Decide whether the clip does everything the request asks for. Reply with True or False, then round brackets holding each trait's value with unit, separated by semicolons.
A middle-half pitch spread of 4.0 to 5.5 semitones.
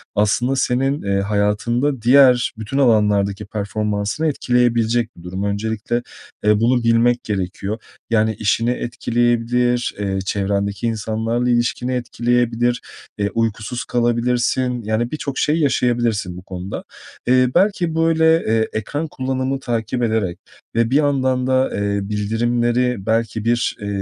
False (2.8 semitones)